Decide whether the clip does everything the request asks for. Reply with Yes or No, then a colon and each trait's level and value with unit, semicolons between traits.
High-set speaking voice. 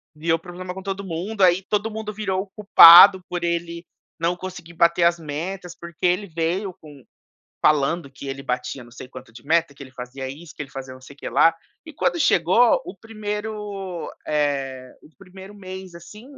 No: medium, 170 Hz